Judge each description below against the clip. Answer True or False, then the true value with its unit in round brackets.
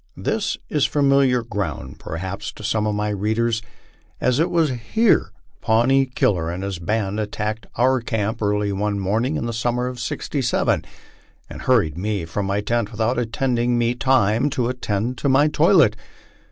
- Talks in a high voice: False (115 Hz)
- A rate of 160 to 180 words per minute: True (165 wpm)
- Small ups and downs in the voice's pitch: False (3.6 semitones)